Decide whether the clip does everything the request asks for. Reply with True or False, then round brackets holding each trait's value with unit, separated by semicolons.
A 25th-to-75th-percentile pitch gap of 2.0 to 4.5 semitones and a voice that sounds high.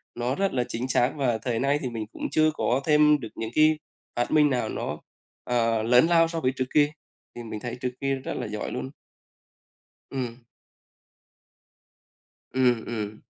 False (3.8 semitones; 125 Hz)